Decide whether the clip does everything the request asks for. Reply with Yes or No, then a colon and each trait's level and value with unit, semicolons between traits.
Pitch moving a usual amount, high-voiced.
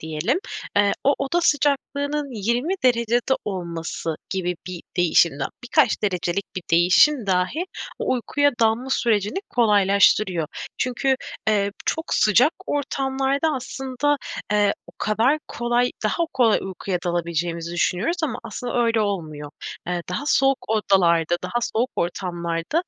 No: wide, 7.0 semitones; high, 215 Hz